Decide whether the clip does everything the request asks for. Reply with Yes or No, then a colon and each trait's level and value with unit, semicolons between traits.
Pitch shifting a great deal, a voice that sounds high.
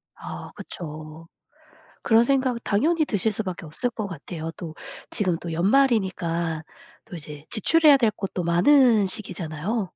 Yes: wide, 6.0 semitones; high, 195 Hz